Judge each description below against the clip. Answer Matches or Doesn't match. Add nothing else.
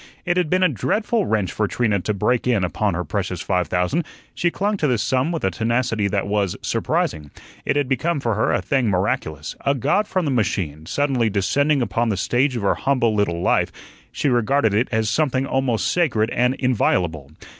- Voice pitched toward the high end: Doesn't match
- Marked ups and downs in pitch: Matches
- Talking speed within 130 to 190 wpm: Doesn't match